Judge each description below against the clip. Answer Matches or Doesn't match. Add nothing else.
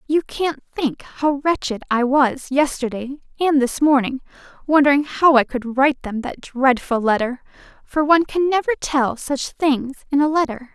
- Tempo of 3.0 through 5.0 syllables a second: Matches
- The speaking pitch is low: Doesn't match